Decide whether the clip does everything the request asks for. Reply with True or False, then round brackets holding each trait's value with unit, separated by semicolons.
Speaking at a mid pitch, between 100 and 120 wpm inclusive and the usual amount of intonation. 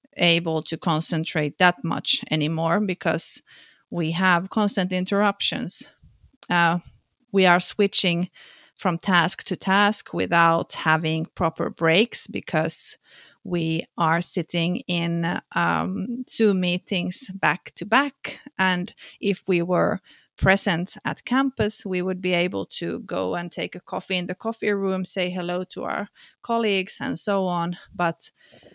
False (180 Hz; 135 wpm; 3.0 semitones)